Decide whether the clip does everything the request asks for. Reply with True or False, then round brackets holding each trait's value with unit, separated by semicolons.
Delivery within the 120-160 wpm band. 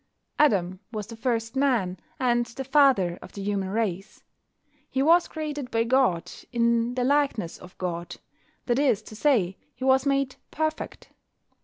True (155 wpm)